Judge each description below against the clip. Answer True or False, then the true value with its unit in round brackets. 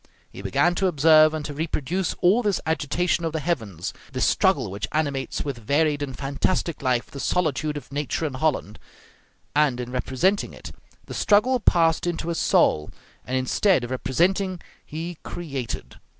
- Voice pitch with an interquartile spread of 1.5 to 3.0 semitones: False (4.7 semitones)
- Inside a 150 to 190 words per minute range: True (165 wpm)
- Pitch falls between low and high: True (150 Hz)